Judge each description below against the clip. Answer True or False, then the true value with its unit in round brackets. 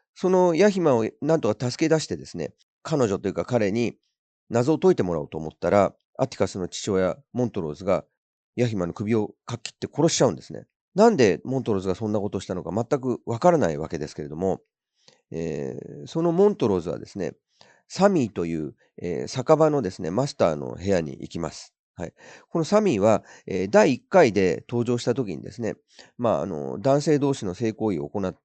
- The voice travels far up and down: True (8.5 semitones)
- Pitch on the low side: True (120 Hz)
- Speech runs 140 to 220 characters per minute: False (395 characters per minute)